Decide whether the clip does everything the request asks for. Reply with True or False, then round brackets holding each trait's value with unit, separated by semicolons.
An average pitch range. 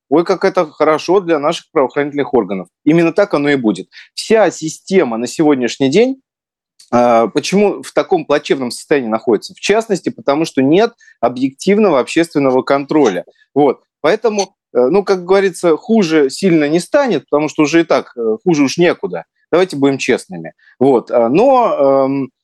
False (6.1 semitones)